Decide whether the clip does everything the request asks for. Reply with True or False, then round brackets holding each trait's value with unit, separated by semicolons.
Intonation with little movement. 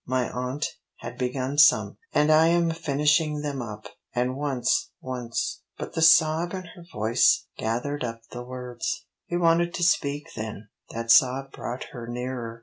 False (4.2 semitones)